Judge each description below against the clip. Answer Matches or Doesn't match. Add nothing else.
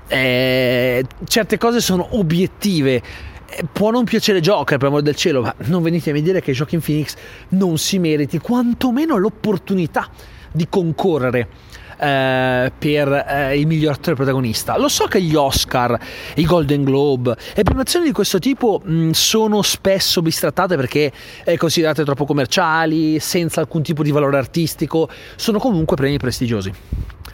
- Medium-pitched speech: Matches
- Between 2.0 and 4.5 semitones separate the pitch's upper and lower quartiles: Doesn't match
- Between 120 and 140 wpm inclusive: Doesn't match